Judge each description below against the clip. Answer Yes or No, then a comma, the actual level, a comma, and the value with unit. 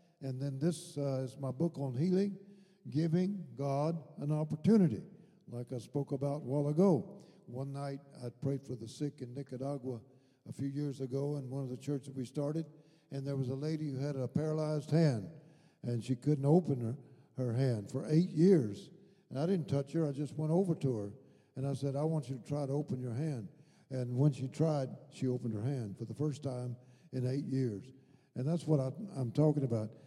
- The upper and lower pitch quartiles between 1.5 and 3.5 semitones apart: Yes, average, 2.9 semitones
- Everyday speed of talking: No, fast, 210 wpm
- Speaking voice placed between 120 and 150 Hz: Yes, medium, 140 Hz